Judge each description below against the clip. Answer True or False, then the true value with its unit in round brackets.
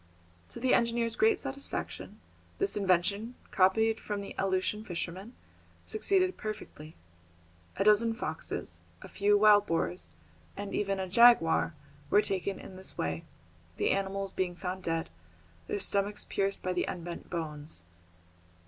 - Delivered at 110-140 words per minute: True (135 wpm)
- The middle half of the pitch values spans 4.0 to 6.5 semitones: False (3.4 semitones)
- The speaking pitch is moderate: False (195 Hz)